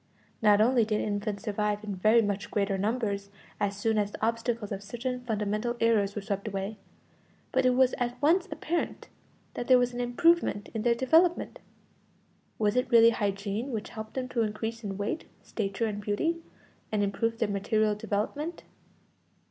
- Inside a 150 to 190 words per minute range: Yes, average, 170 wpm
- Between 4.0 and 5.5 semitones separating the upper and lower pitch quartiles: No, average, 3.0 semitones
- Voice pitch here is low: No, high, 220 Hz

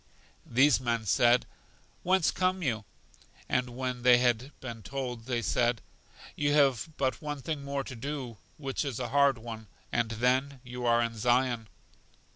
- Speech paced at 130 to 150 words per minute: No, average, 160 wpm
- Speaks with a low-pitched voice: Yes, low, 125 Hz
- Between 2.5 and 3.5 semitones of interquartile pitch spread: Yes, average, 2.8 semitones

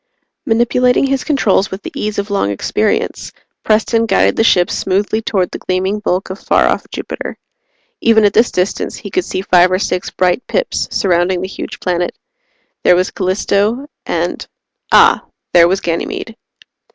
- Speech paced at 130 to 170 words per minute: Yes, average, 165 wpm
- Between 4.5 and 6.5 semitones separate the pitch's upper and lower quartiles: No, average, 3.5 semitones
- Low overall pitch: No, high, 195 Hz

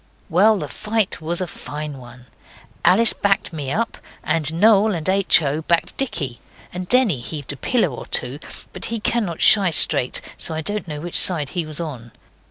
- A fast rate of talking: No, average, 190 wpm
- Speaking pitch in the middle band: Yes, medium, 170 Hz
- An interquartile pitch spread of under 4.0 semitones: No, wide, 5.5 semitones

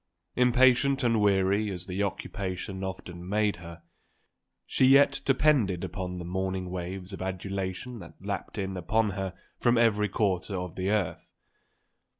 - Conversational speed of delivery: Yes, average, 145 wpm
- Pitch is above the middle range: No, very low, 95 Hz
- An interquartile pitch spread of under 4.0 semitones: Yes, average, 2.9 semitones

